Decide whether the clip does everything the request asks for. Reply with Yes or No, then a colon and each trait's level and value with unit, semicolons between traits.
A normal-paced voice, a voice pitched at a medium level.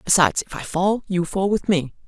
No: fast, 230 wpm; medium, 180 Hz